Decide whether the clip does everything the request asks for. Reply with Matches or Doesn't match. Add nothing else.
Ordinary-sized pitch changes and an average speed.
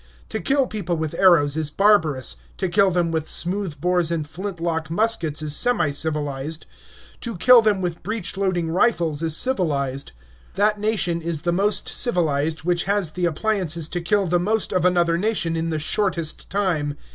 Matches